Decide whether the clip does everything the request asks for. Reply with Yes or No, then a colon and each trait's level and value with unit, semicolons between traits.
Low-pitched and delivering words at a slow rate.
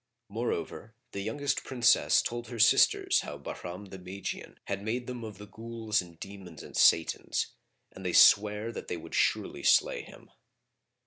No: low, 105 Hz; average, 165 wpm